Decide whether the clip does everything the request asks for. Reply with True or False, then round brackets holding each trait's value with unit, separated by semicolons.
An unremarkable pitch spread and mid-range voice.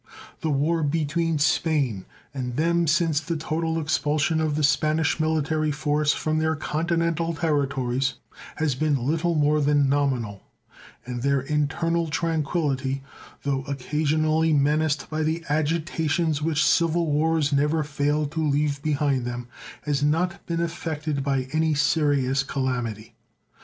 False (2.2 semitones; 150 Hz)